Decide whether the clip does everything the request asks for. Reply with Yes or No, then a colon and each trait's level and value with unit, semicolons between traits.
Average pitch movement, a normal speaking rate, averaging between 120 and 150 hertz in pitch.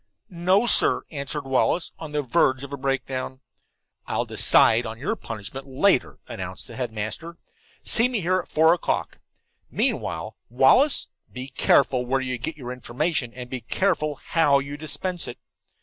Yes: average, 4.7 semitones; average, 150 wpm; medium, 140 Hz